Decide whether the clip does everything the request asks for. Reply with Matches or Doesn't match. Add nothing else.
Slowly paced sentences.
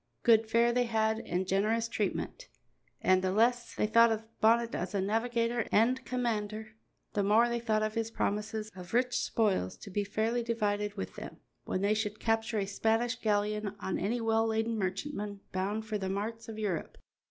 Doesn't match